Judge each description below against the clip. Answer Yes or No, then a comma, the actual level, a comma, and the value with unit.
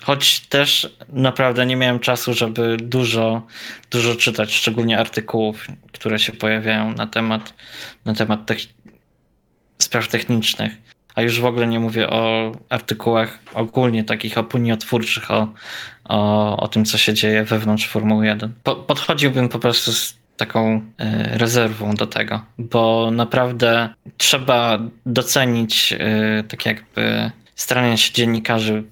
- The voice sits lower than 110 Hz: No, low, 115 Hz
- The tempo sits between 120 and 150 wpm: Yes, average, 130 wpm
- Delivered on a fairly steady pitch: Yes, narrow, 1.7 semitones